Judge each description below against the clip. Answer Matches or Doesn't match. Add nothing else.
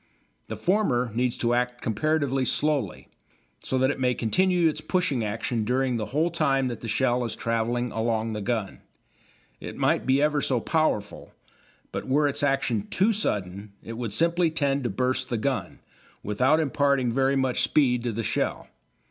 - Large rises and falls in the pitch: Doesn't match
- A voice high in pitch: Doesn't match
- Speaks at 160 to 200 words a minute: Matches